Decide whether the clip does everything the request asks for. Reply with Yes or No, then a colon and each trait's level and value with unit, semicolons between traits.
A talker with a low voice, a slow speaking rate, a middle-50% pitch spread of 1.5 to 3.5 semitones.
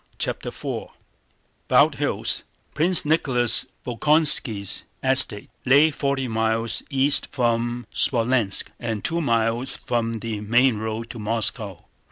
Yes: low, 120 Hz; slow, 115 wpm; average, 3.2 semitones